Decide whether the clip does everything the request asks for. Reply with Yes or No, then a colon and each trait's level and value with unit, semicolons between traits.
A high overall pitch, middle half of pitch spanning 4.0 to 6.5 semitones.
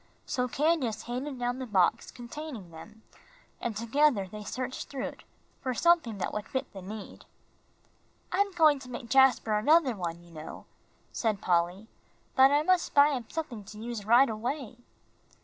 Yes: high, 240 Hz; average, 4.8 semitones